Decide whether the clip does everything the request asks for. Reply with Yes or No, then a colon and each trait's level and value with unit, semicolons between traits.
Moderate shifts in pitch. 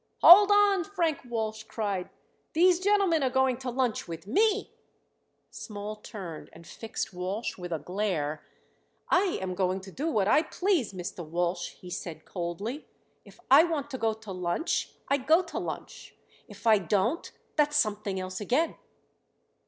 No: wide, 8.9 semitones